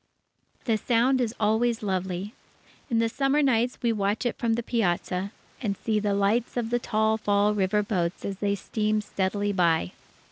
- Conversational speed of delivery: Yes, average, 175 wpm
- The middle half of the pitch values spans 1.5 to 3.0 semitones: Yes, narrow, 2.6 semitones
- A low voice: No, high, 215 Hz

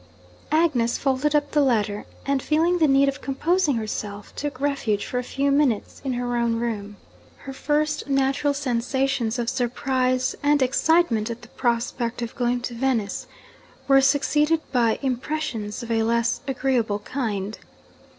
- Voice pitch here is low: No, very high, 255 Hz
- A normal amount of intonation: Yes, average, 3.3 semitones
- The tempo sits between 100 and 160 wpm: Yes, average, 150 wpm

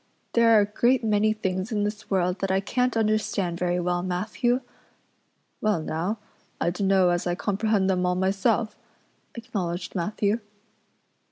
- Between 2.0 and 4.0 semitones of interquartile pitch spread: Yes, average, 3.2 semitones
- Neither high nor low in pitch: No, high, 195 Hz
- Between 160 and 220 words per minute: No, average, 150 wpm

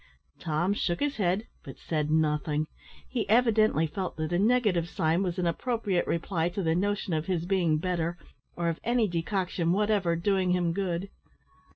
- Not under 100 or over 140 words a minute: No, average, 170 wpm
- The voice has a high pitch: No, medium, 175 Hz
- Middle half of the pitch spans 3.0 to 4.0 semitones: Yes, average, 3.3 semitones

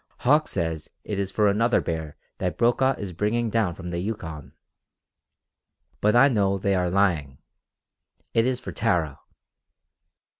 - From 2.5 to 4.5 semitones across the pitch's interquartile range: No, average, 5.0 semitones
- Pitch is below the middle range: Yes, low, 100 Hz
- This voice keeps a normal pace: Yes, average, 145 wpm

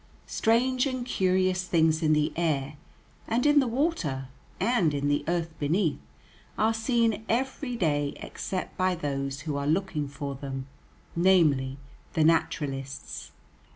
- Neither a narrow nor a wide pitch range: No, wide, 7.4 semitones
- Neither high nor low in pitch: Yes, medium, 165 Hz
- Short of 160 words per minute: Yes, slow, 135 wpm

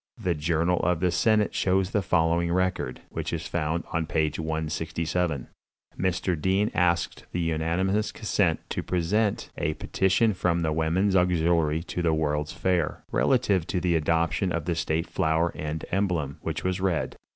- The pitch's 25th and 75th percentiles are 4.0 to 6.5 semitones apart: No, narrow, 2.6 semitones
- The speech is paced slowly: No, average, 160 wpm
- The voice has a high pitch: No, very low, 85 Hz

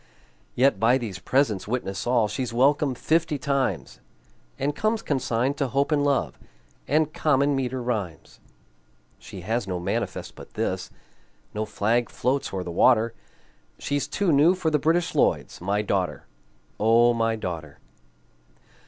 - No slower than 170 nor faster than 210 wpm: No, average, 145 wpm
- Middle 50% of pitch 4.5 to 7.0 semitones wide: Yes, average, 5.1 semitones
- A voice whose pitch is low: Yes, low, 125 Hz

